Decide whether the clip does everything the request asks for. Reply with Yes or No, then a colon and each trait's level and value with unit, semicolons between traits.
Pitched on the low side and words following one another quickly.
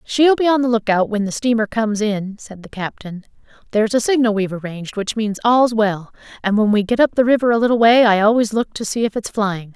No: high, 220 Hz; fast, 245 wpm